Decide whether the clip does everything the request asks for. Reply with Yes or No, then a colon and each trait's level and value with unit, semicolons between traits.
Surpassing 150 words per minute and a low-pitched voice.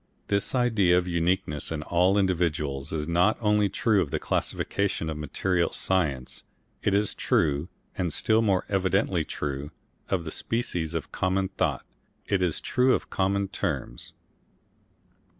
No: average, 145 wpm; very low, 90 Hz